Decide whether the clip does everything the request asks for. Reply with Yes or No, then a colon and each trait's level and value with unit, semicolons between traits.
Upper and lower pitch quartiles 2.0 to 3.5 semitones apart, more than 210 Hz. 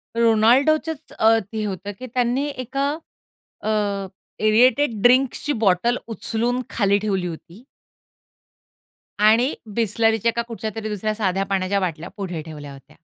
No: average, 3.9 semitones; high, 220 Hz